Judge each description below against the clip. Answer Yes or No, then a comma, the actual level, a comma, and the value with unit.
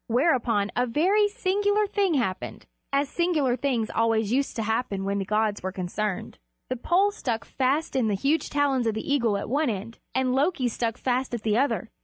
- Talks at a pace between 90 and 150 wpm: No, average, 200 wpm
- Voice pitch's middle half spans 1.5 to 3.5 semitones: No, average, 4.9 semitones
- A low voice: No, very high, 250 Hz